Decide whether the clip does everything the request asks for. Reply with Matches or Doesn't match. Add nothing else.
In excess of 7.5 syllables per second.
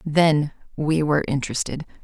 Doesn't match